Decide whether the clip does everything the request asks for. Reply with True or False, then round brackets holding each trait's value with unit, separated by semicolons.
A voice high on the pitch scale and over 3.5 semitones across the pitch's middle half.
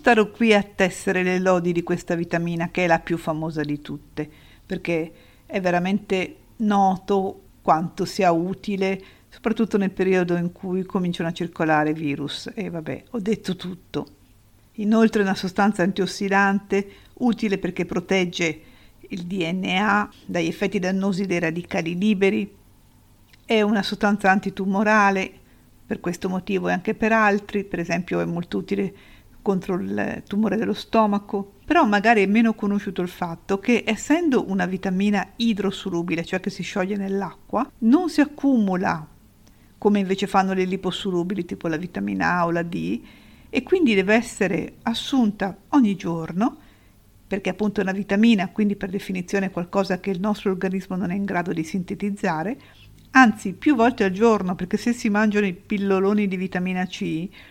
False (195 Hz; 2.8 semitones)